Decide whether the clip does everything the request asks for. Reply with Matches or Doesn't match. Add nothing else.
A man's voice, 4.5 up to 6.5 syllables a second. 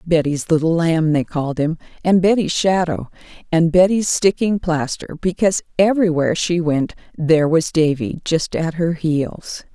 Doesn't match